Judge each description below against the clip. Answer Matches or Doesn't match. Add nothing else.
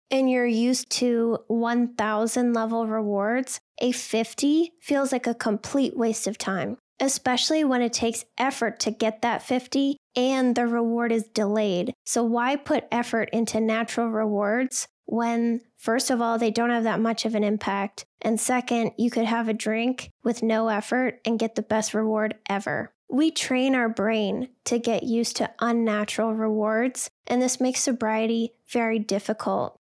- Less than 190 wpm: Matches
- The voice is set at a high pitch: Matches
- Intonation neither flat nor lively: Doesn't match